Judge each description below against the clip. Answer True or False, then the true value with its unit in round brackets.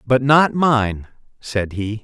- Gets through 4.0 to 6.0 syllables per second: False (3.1 syllables/s)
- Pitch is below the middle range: True (120 Hz)